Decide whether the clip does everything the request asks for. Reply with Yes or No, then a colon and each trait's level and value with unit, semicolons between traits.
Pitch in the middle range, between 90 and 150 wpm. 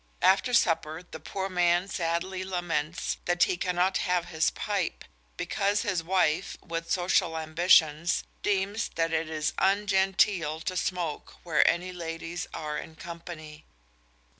Yes: medium, 175 Hz; slow, 135 wpm